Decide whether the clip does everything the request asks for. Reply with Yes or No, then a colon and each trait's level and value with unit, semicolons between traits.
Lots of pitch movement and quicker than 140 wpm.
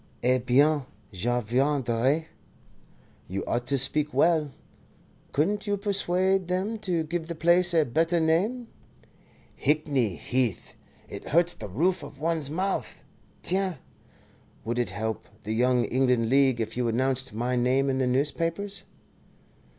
No: wide, 5.7 semitones; slow, 135 wpm